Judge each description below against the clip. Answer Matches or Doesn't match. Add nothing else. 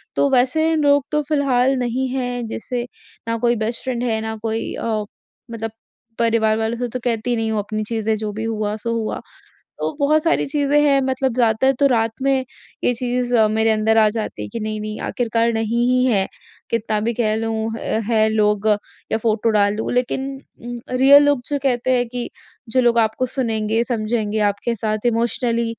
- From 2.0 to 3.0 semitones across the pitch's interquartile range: Matches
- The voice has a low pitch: Doesn't match